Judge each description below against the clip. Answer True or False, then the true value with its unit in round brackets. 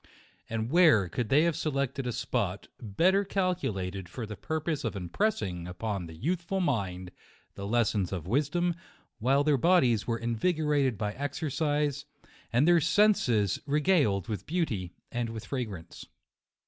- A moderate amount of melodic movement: False (7.4 semitones)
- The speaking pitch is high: False (125 Hz)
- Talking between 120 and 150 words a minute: True (145 wpm)